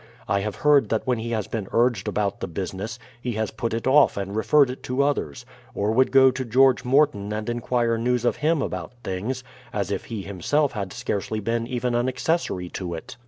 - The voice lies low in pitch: Yes, low, 115 Hz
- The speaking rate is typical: No, fast, 215 wpm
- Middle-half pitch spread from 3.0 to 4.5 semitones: Yes, average, 4.1 semitones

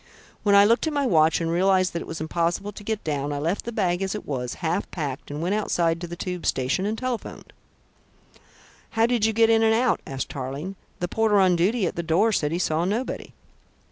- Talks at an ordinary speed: No, fast, 230 wpm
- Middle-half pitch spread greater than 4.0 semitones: Yes, average, 4.9 semitones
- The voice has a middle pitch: Yes, medium, 180 Hz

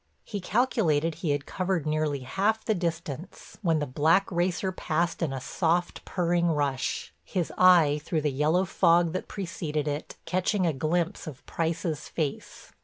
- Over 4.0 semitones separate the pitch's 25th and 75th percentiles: No, average, 3.2 semitones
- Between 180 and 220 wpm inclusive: No, average, 160 wpm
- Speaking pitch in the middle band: Yes, medium, 165 Hz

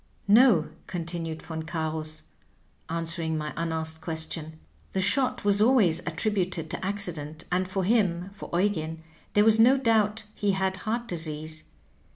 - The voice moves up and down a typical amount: Yes, average, 4.4 semitones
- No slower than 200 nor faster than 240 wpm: No, average, 140 wpm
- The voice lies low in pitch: No, medium, 175 Hz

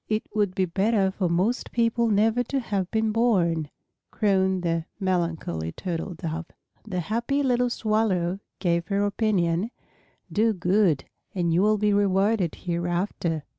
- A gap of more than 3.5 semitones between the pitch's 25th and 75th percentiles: Yes, average, 3.9 semitones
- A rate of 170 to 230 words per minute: No, average, 140 wpm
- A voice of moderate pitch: No, high, 195 Hz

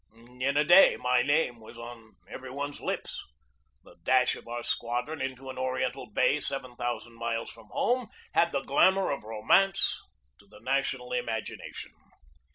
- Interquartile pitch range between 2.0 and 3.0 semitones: No, average, 3.5 semitones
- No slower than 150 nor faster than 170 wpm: Yes, average, 165 wpm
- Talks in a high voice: No, low, 130 Hz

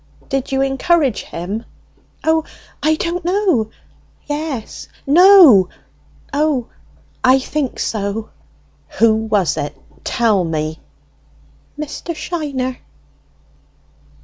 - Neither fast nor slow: No, slow, 95 wpm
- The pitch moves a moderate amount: No, wide, 6.3 semitones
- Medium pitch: No, very high, 265 Hz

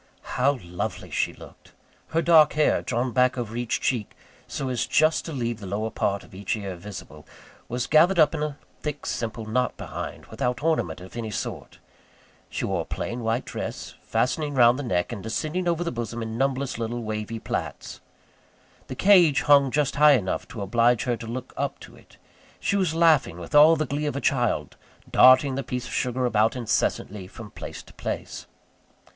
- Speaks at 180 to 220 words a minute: Yes, average, 190 wpm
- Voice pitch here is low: Yes, low, 125 Hz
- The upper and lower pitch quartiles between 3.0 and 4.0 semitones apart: No, average, 4.7 semitones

